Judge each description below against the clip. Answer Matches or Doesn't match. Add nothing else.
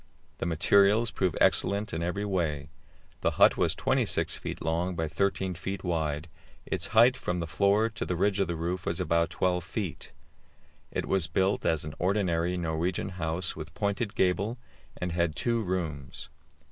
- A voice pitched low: Matches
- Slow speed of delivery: Doesn't match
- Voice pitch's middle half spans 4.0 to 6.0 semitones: Doesn't match